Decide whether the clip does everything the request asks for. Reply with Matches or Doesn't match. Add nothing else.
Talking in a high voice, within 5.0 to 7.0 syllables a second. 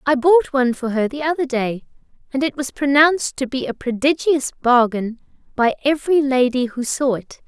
Matches